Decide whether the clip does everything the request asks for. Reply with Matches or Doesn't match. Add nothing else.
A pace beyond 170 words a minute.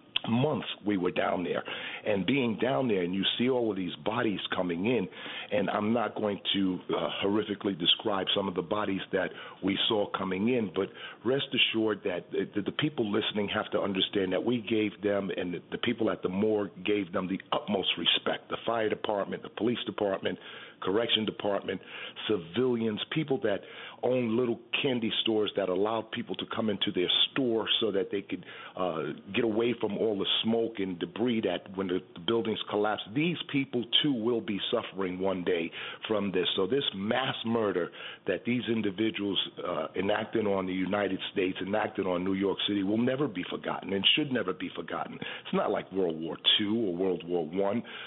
Matches